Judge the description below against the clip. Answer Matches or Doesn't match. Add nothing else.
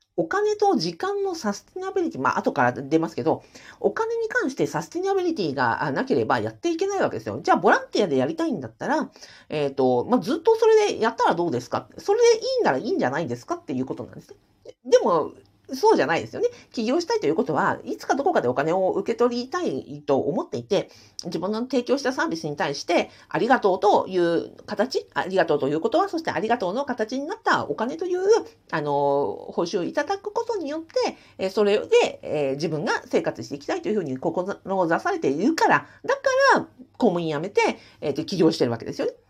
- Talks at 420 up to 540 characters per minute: Matches